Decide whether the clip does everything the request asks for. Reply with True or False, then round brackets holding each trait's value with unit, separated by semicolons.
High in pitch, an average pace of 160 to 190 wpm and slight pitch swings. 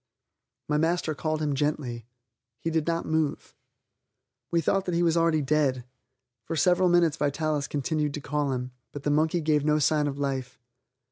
False (150 Hz; 175 wpm; 2.3 semitones)